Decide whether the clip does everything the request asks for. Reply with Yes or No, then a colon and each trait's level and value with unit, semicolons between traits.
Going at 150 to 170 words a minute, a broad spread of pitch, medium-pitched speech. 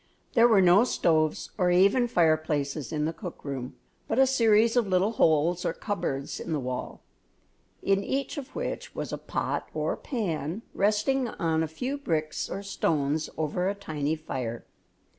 Yes: average, 165 wpm; wide, 5.8 semitones; medium, 175 Hz